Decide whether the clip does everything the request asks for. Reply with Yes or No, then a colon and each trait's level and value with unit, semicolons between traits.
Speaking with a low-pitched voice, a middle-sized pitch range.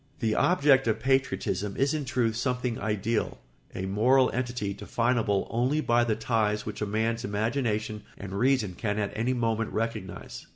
Yes: low, 115 Hz; average, 3.1 semitones